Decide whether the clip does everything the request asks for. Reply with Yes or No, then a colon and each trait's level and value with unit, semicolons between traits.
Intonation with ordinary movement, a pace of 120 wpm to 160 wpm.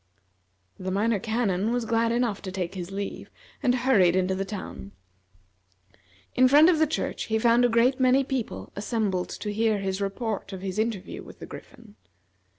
No: average, 4.1 semitones; average, 175 wpm